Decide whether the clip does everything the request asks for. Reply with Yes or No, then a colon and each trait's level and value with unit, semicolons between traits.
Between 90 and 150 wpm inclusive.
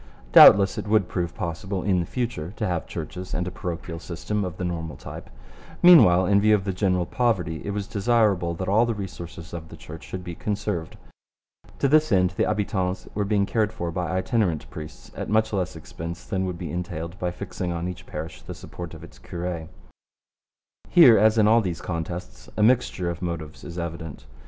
No: average, 200 wpm